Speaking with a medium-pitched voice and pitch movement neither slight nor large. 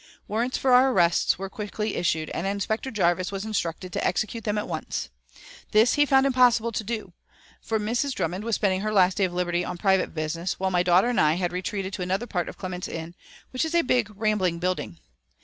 No: high, 195 Hz; average, 4.0 semitones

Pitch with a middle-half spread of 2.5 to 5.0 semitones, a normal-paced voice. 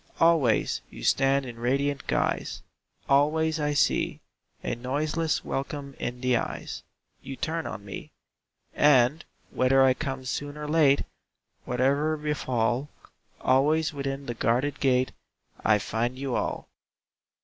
No: average, 2.8 semitones; slow, 125 wpm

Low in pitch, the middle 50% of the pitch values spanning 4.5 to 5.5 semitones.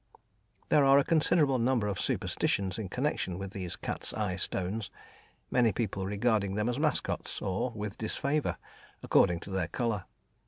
Yes: low, 105 Hz; average, 4.9 semitones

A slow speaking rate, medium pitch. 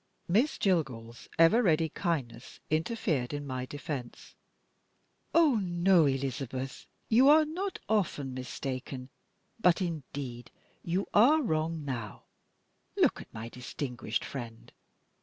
Yes: slow, 110 wpm; medium, 150 Hz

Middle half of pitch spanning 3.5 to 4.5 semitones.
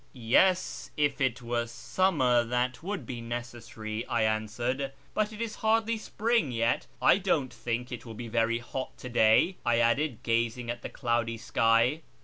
Yes: average, 4.0 semitones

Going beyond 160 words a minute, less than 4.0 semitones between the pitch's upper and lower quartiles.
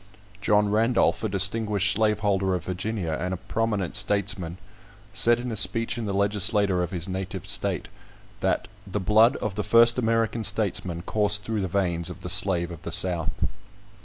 Yes: average, 170 wpm; average, 2.9 semitones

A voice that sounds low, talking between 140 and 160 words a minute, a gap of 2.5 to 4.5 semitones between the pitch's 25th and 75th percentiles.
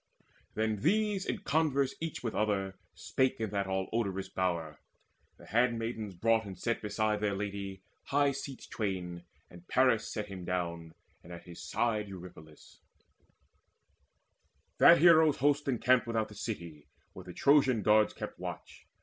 No: low, 105 Hz; average, 150 wpm; average, 4.9 semitones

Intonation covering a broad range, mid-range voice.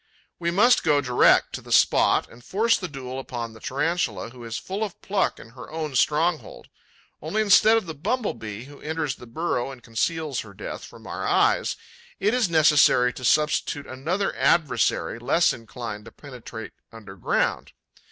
Yes: wide, 6.2 semitones; medium, 145 Hz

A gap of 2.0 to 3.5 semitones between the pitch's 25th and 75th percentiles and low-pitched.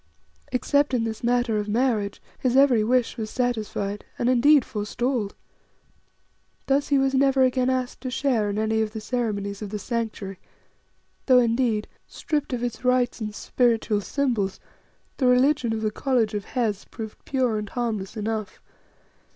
No: average, 3.2 semitones; high, 235 Hz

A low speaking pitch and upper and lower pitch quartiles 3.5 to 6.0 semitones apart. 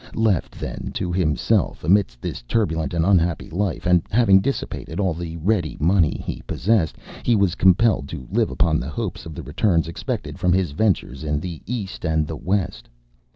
Yes: very low, 85 Hz; average, 3.8 semitones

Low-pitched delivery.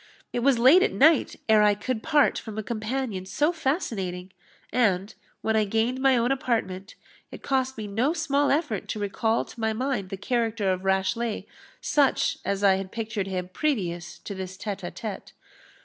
No: high, 220 Hz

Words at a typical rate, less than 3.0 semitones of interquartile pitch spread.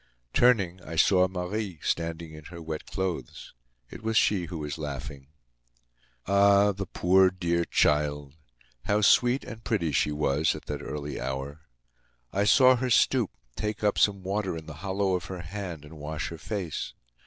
No: average, 165 wpm; average, 4.7 semitones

